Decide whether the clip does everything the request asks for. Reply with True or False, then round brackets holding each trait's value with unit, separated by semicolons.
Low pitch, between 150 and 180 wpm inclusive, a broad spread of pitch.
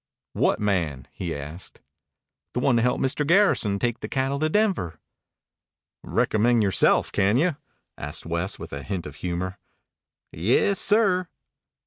False (105 Hz; 140 wpm; 8.4 semitones)